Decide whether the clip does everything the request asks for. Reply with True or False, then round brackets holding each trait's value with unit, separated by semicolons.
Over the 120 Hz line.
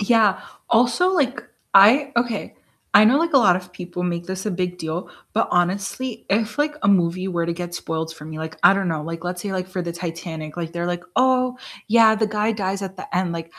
True (185 Hz)